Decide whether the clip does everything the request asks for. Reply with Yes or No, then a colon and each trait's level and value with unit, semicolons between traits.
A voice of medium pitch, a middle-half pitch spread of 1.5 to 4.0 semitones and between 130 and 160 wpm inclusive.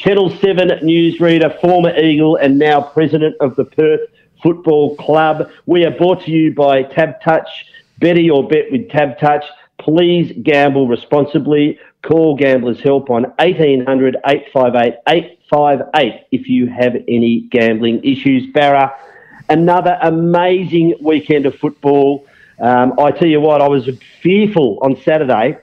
Yes: medium, 150 Hz; average, 3.2 semitones; average, 140 wpm